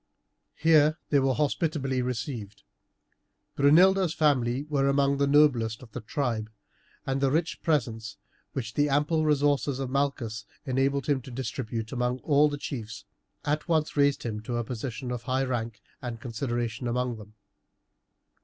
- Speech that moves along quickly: No, average, 150 wpm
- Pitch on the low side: Yes, low, 130 Hz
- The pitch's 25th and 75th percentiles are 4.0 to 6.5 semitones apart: No, average, 3.5 semitones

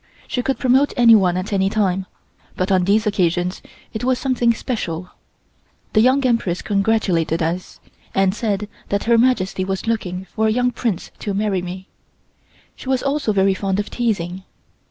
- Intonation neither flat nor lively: Yes, average, 3.9 semitones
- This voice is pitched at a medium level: No, high, 200 Hz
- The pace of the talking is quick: No, average, 165 wpm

